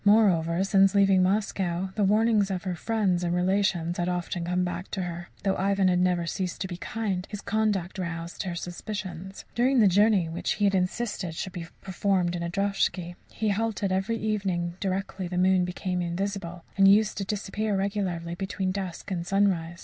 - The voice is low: No, high, 190 Hz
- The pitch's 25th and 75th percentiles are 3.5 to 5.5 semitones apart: No, narrow, 2.4 semitones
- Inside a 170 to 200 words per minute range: Yes, average, 185 wpm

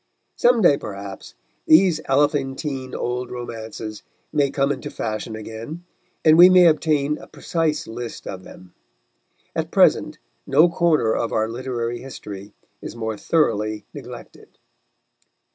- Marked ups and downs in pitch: Yes, wide, 5.7 semitones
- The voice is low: Yes, low, 130 Hz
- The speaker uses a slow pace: Yes, slow, 125 wpm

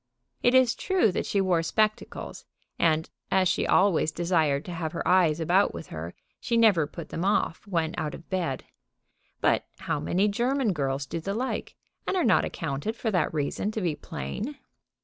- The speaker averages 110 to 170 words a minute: No, average, 185 wpm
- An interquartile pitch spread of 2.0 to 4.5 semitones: No, average, 4.9 semitones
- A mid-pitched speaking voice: Yes, medium, 180 Hz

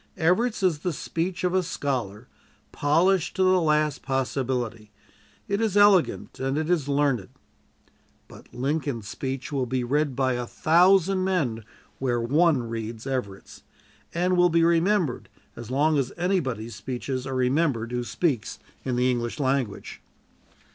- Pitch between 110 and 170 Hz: Yes, medium, 140 Hz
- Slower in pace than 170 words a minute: Yes, average, 145 wpm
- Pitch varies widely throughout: Yes, wide, 5.7 semitones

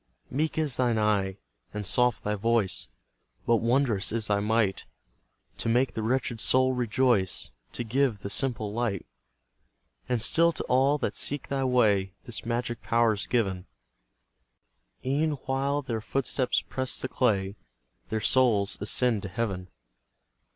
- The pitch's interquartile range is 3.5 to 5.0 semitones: Yes, average, 3.9 semitones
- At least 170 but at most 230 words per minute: No, average, 145 wpm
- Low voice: Yes, low, 115 Hz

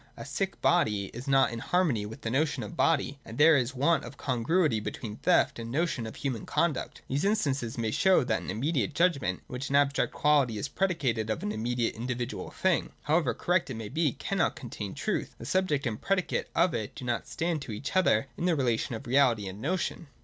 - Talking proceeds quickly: Yes, fast, 220 wpm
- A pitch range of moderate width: No, wide, 6.1 semitones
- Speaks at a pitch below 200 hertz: Yes, low, 135 Hz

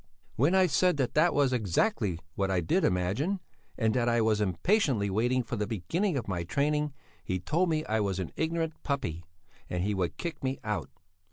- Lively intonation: Yes, wide, 7.9 semitones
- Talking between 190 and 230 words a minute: Yes, average, 195 wpm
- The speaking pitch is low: Yes, low, 120 Hz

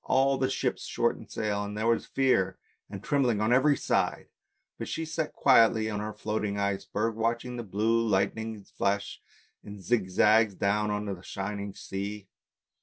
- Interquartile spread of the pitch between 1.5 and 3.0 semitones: Yes, narrow, 2.5 semitones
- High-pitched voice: No, low, 105 Hz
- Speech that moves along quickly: No, average, 170 wpm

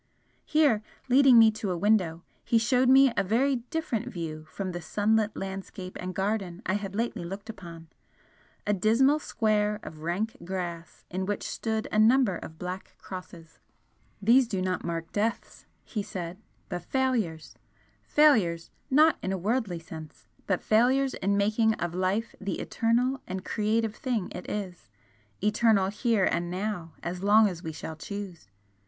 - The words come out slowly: No, average, 160 wpm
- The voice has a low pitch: No, high, 205 Hz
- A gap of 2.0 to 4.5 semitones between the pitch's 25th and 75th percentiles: Yes, average, 4.1 semitones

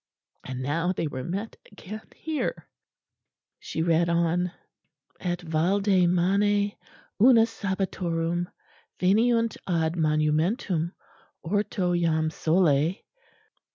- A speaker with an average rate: No, slow, 90 wpm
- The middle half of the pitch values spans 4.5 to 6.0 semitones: No, average, 3.6 semitones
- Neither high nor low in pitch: Yes, medium, 175 Hz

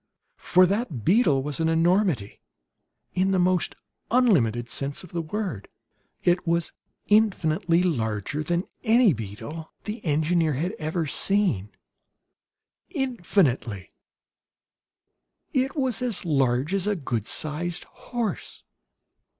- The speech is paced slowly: Yes, slow, 110 wpm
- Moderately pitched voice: Yes, medium, 170 Hz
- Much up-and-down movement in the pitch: Yes, wide, 5.9 semitones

